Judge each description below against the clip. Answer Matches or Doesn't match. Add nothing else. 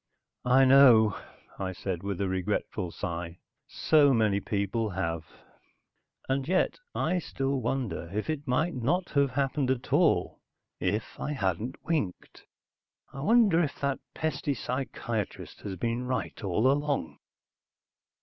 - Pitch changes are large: Matches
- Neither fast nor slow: Doesn't match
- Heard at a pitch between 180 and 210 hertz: Doesn't match